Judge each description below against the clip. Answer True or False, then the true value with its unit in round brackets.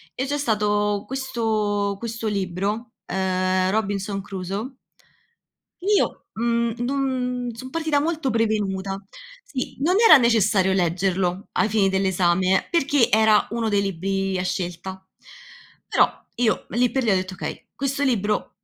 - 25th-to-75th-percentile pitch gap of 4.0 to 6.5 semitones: True (4.3 semitones)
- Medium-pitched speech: False (210 Hz)